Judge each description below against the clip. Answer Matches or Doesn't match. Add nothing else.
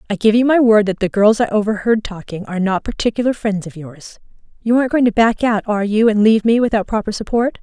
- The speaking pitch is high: Matches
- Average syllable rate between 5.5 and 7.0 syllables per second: Matches